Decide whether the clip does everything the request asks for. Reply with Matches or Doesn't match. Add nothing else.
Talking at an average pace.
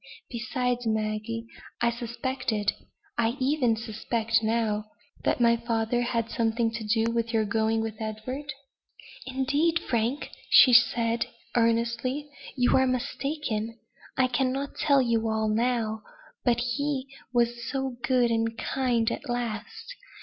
Doesn't match